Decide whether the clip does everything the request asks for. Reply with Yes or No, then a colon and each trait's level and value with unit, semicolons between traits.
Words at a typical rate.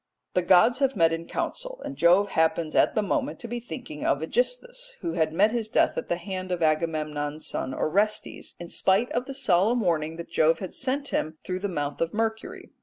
No: fast, 210 wpm